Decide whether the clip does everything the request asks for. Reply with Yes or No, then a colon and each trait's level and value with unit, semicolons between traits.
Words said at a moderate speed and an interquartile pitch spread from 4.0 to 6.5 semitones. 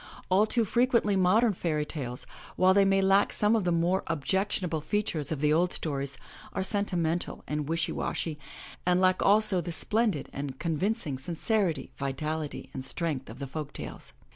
Yes: average, 170 wpm; average, 4.7 semitones